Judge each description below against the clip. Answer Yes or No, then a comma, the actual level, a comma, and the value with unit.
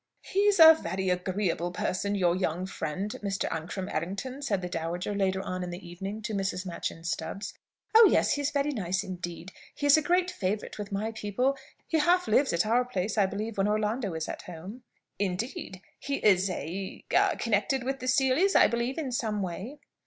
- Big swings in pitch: Yes, wide, 5.7 semitones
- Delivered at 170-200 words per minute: Yes, average, 190 wpm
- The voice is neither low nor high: No, high, 200 Hz